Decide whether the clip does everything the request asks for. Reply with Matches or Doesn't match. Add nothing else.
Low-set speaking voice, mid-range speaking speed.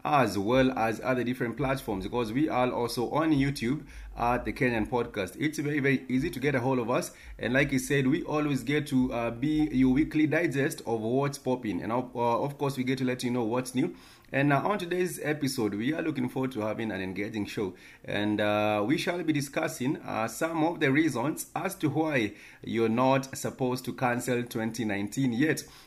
Doesn't match